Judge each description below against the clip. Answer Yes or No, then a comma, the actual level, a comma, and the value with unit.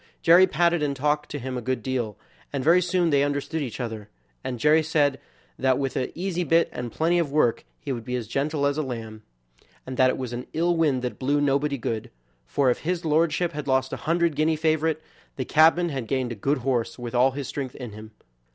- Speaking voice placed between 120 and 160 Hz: Yes, medium, 140 Hz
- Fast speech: Yes, fast, 225 wpm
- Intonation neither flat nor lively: Yes, average, 4.0 semitones